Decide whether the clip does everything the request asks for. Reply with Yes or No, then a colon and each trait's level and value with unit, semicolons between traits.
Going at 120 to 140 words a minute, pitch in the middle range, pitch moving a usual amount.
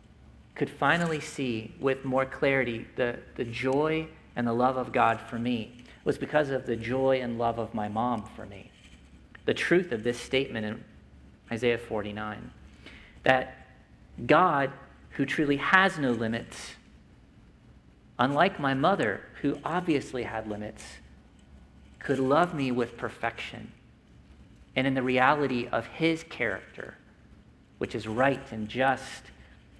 No: slow, 135 wpm; low, 125 Hz; average, 3.6 semitones